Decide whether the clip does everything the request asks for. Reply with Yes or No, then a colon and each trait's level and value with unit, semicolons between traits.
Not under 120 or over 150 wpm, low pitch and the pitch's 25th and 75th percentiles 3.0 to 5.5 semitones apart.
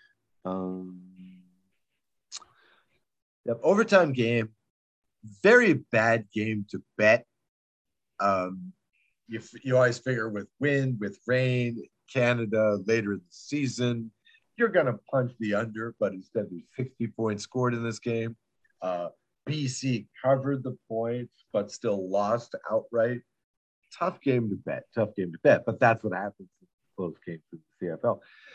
Yes: slow, 135 wpm; low, 115 Hz; average, 3.7 semitones